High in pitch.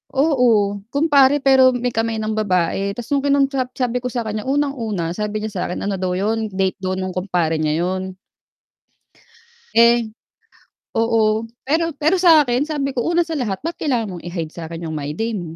Yes: high, 225 Hz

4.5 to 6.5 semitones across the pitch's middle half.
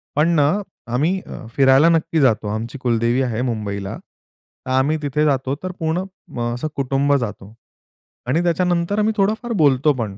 Yes: average, 5.2 semitones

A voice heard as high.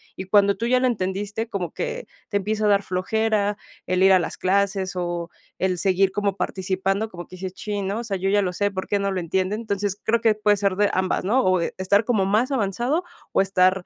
Yes: high, 200 Hz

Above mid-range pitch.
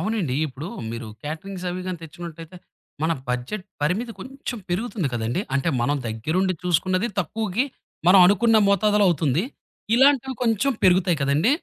No: medium, 180 Hz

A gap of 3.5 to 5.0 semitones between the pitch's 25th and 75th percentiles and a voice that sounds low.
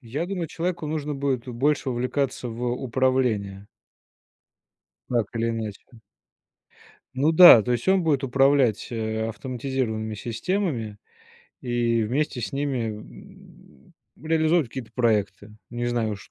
Yes: average, 4.0 semitones; low, 125 Hz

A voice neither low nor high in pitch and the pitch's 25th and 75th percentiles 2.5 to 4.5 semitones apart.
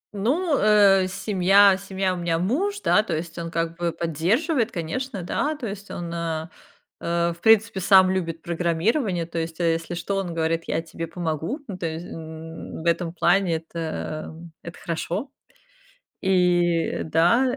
Yes: medium, 175 Hz; average, 3.2 semitones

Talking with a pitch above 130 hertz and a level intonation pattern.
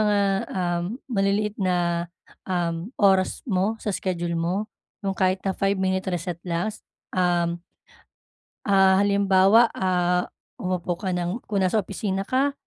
Yes: high, 190 Hz; narrow, 2.2 semitones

